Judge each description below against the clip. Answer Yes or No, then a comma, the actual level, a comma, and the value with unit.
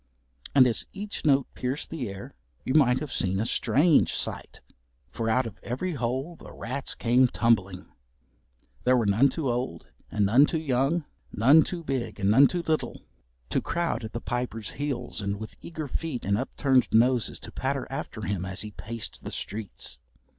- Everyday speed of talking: Yes, average, 180 wpm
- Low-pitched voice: Yes, low, 125 Hz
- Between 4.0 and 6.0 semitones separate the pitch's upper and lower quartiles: Yes, average, 4.7 semitones